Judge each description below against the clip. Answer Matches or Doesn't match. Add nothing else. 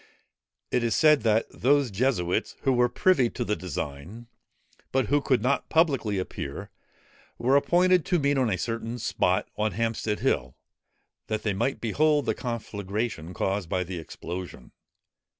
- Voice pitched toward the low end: Matches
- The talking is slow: Doesn't match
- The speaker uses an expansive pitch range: Matches